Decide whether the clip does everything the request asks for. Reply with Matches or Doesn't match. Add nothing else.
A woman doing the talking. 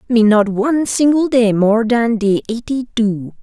Matches